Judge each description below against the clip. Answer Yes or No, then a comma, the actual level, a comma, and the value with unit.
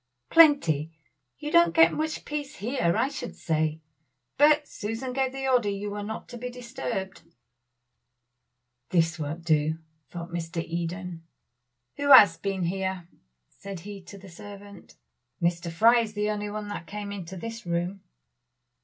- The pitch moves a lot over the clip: Yes, wide, 6.2 semitones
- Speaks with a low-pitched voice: No, high, 200 Hz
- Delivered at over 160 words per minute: No, average, 150 wpm